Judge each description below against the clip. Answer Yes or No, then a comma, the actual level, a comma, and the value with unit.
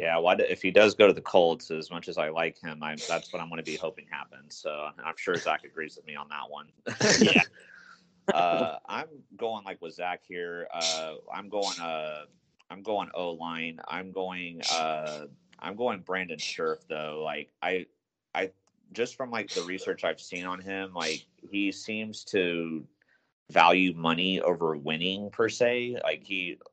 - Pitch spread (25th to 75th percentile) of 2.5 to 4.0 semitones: Yes, average, 3.3 semitones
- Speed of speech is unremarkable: Yes, average, 185 wpm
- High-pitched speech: No, very low, 85 Hz